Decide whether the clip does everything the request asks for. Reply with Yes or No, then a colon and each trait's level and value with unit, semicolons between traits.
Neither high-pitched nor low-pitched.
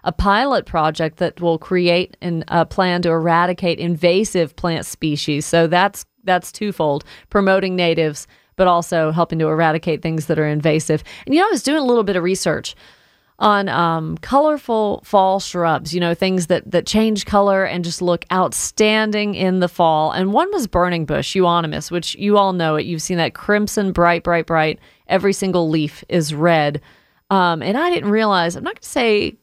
Yes: medium, 175 Hz